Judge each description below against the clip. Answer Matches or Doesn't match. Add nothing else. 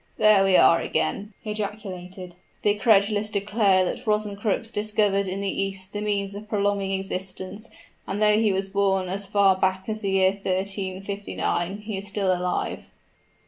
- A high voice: Matches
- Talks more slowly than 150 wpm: Doesn't match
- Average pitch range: Doesn't match